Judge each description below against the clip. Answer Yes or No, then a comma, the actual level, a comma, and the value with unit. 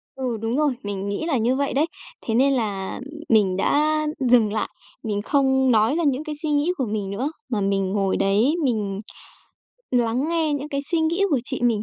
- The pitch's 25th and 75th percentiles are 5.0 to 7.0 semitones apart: Yes, wide, 5.6 semitones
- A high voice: Yes, very high, 250 Hz